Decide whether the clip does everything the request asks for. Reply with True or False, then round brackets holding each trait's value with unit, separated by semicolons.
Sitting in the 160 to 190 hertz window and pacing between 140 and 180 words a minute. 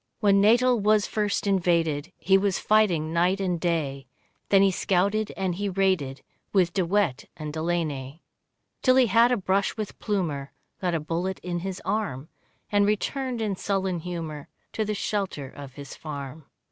True (185 Hz; 165 wpm)